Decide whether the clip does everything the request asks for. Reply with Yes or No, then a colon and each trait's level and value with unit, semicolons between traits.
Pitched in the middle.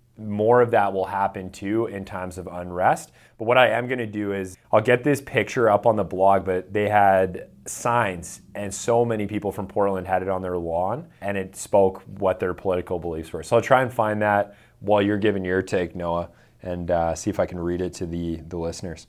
No: low, 100 Hz